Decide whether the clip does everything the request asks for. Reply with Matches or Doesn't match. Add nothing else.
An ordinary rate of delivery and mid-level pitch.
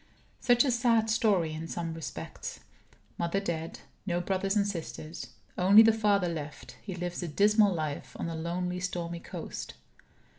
Matches